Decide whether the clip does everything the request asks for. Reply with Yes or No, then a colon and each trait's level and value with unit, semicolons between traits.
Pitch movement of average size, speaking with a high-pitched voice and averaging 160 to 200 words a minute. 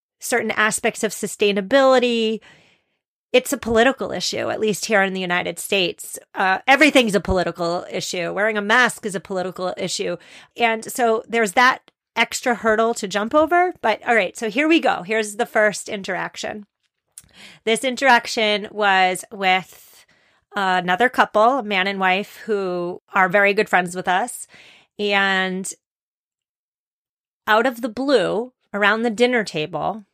No: average, 4.0 semitones; high, 215 Hz; average, 145 wpm